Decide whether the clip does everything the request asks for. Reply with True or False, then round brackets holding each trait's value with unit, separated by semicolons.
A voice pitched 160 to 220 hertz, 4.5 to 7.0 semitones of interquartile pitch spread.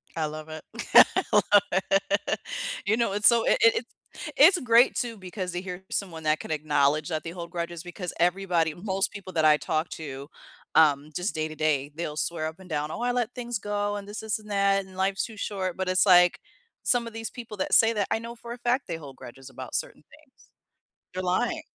True (185 Hz; 5.1 semitones)